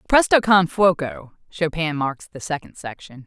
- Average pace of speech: Yes, average, 145 wpm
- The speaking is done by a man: No, female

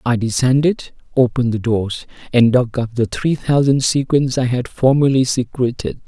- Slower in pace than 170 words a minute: Yes, average, 160 wpm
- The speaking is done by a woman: No, male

